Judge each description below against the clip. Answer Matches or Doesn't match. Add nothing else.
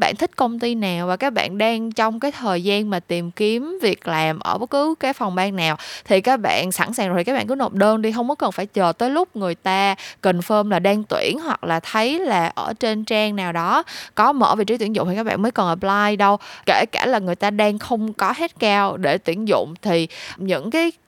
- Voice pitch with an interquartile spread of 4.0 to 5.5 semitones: Matches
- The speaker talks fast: Matches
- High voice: Matches